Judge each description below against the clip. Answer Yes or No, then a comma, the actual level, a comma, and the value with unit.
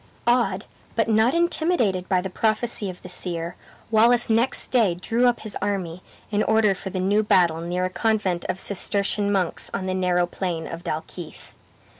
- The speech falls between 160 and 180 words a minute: Yes, average, 175 wpm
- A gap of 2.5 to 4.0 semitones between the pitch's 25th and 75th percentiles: Yes, average, 3.6 semitones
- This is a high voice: Yes, high, 195 Hz